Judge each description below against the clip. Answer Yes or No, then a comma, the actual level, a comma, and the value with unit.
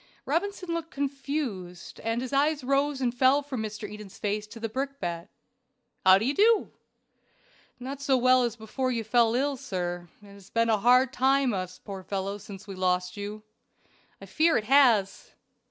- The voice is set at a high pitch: Yes, high, 235 Hz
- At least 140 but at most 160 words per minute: No, average, 175 wpm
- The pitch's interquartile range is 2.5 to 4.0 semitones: No, wide, 5.4 semitones